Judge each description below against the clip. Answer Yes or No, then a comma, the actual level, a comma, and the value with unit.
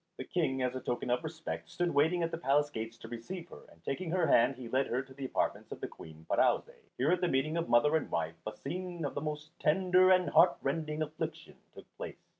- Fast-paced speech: Yes, fast, 240 wpm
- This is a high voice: No, medium, 150 Hz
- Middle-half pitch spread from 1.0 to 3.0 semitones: No, average, 5.0 semitones